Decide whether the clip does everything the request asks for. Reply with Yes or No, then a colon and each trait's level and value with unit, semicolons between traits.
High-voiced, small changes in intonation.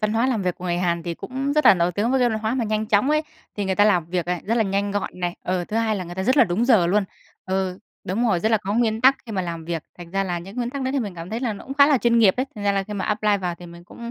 No: high, 205 Hz; average, 4.5 semitones